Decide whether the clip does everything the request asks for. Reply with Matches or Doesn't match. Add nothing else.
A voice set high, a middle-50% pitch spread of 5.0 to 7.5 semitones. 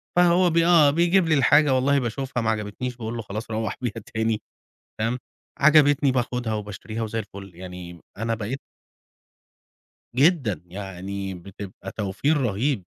Doesn't match